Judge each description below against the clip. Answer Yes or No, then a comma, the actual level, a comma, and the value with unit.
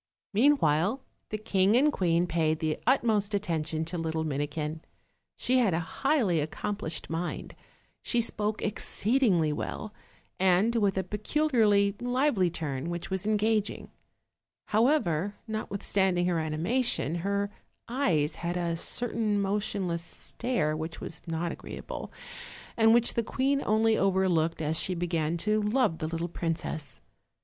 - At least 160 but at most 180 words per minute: No, average, 140 wpm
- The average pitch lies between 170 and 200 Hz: Yes, high, 190 Hz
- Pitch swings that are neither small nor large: Yes, average, 5.0 semitones